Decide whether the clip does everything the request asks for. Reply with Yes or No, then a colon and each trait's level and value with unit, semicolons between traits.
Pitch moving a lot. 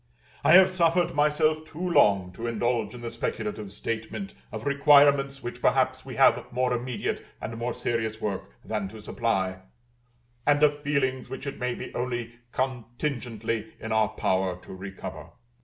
No: average, 4.4 semitones